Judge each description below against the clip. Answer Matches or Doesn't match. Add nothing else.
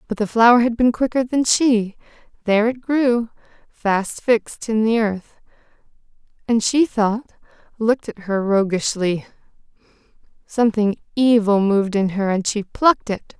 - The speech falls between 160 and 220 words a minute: Doesn't match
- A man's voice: Doesn't match